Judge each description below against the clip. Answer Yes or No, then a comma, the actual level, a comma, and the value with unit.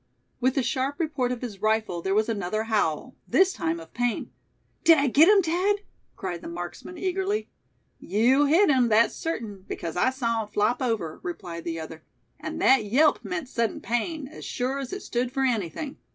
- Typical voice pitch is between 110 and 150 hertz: No, high, 240 Hz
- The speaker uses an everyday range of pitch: No, wide, 5.7 semitones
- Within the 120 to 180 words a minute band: No, average, 190 wpm